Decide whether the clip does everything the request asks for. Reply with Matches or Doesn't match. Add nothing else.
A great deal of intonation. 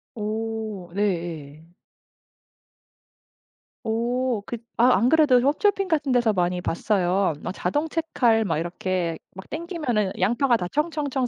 Matches